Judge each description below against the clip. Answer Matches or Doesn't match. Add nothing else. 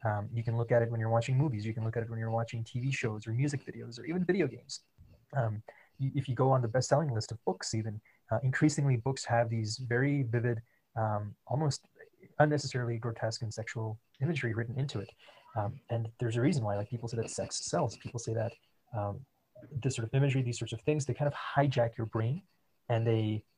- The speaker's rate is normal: Doesn't match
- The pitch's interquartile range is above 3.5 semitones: Doesn't match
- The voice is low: Matches